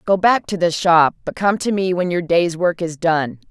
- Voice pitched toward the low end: No, medium, 175 Hz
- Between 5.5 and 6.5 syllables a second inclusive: No, 4.6 syllables/s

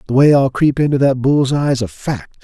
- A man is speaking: Yes, male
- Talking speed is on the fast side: Yes, fast, 245 wpm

